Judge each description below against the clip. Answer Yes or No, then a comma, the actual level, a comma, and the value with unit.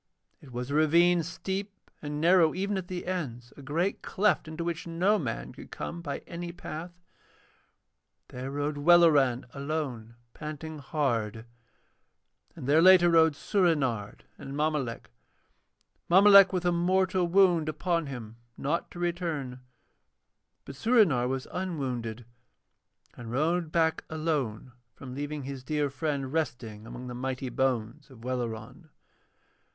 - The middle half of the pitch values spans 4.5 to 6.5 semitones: Yes, average, 5.0 semitones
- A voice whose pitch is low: No, medium, 150 Hz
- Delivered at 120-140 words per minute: Yes, slow, 135 wpm